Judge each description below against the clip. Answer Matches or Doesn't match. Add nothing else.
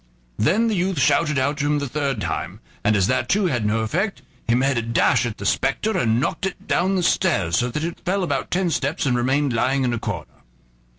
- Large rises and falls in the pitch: Matches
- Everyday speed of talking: Doesn't match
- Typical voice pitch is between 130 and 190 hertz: Matches